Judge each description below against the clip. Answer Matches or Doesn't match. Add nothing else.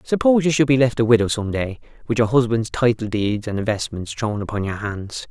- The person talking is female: Doesn't match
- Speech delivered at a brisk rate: Matches